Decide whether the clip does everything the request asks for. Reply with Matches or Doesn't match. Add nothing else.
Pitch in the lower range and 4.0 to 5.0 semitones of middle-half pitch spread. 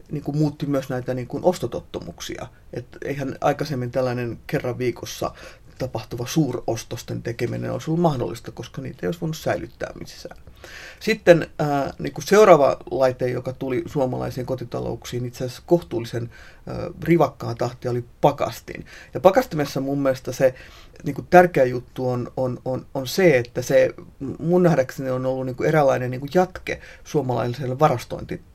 Matches